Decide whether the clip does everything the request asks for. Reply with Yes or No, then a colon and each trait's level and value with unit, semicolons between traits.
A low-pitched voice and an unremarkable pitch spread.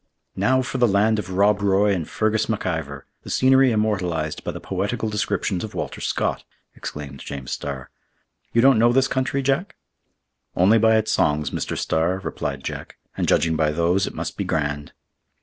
No: low, 100 Hz; wide, 5.8 semitones